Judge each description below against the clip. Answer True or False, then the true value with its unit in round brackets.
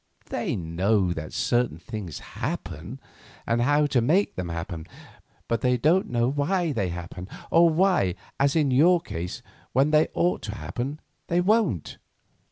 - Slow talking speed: False (155 wpm)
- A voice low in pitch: True (125 Hz)